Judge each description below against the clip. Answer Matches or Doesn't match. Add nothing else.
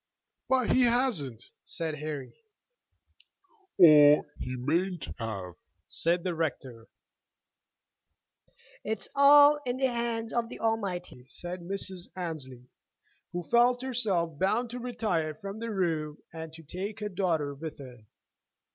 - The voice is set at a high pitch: Doesn't match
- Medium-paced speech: Doesn't match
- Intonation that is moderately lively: Doesn't match